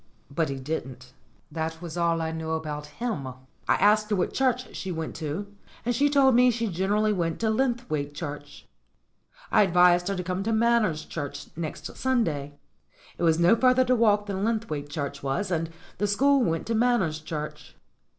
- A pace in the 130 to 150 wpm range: No, average, 180 wpm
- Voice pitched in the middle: Yes, medium, 180 Hz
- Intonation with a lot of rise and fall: Yes, wide, 6.4 semitones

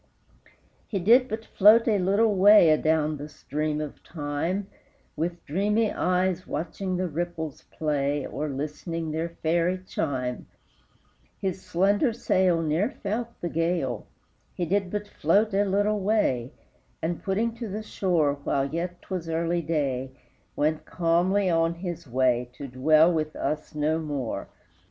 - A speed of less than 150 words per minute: Yes, average, 140 wpm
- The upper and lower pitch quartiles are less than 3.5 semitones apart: No, average, 4.3 semitones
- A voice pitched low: No, medium, 170 Hz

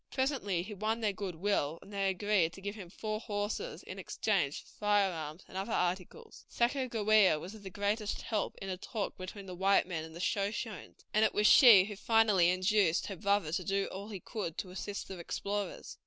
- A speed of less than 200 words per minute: No, fast, 205 wpm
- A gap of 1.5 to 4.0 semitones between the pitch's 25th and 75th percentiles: Yes, narrow, 2.6 semitones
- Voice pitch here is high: Yes, high, 200 Hz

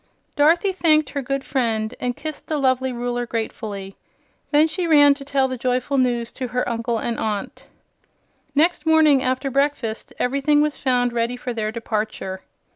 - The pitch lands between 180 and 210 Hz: No, very high, 255 Hz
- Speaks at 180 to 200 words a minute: No, average, 165 wpm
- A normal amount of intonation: Yes, average, 3.6 semitones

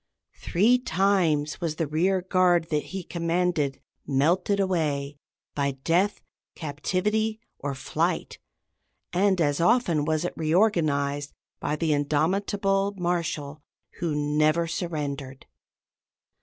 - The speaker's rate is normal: No, slow, 105 wpm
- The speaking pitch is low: No, medium, 165 Hz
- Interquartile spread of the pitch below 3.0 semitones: No, average, 4.0 semitones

